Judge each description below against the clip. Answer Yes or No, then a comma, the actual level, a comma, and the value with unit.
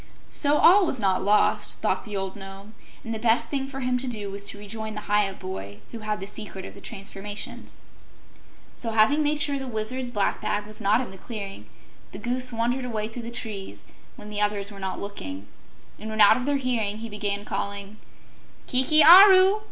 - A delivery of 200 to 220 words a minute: Yes, fast, 205 wpm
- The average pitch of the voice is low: No, high, 215 Hz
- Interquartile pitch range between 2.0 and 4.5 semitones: Yes, average, 3.8 semitones